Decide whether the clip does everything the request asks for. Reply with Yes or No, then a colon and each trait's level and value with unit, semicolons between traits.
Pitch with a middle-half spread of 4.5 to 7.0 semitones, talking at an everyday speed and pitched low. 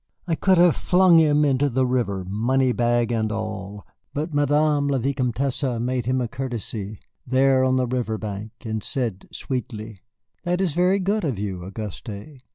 Yes: average, 4.8 semitones; average, 165 wpm; low, 125 Hz